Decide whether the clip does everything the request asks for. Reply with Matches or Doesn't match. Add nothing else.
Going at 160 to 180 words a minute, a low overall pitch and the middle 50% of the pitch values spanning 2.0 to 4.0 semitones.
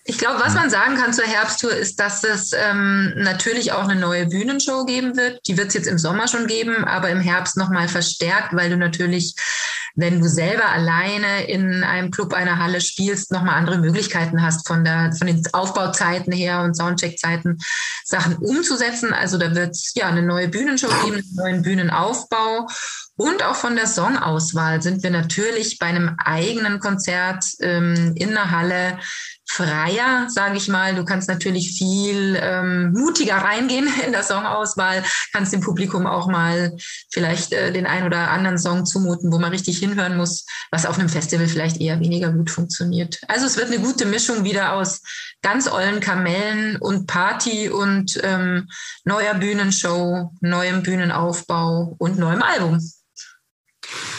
Doesn't match